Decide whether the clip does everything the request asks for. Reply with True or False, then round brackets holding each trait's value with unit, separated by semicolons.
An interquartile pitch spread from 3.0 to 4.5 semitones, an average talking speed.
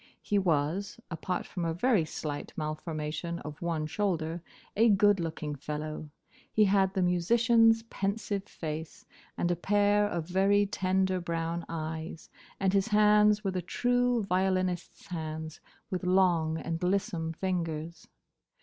False (3.8 semitones; 130 wpm)